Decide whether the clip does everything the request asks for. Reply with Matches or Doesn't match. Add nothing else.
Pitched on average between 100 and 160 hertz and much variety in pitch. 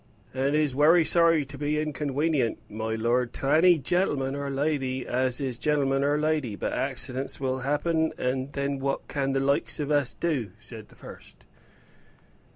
Doesn't match